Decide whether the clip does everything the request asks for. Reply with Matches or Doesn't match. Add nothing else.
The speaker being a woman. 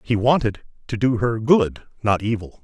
Doesn't match